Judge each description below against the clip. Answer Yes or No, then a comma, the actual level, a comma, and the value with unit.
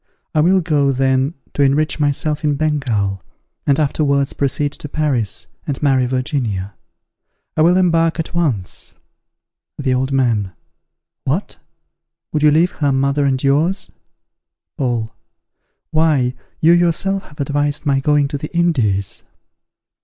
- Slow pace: Yes, slow, 130 wpm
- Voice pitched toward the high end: No, medium, 145 Hz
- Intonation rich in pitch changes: No, average, 2.9 semitones